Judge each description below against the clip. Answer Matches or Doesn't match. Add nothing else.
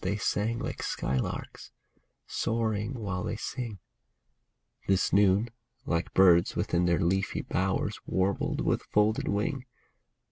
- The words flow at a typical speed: Doesn't match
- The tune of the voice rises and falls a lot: Doesn't match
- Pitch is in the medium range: Doesn't match